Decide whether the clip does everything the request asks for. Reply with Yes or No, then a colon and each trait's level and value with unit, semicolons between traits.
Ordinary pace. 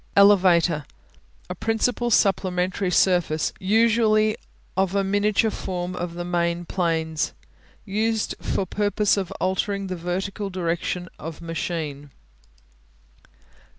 No: slow, 105 wpm